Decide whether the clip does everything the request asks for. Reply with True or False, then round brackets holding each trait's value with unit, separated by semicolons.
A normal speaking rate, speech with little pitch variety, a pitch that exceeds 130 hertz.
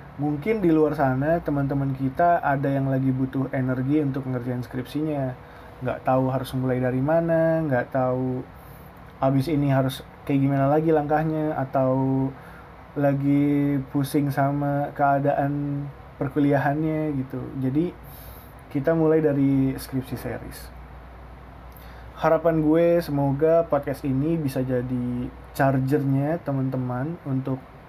True (110 wpm; 2.3 semitones; 140 Hz)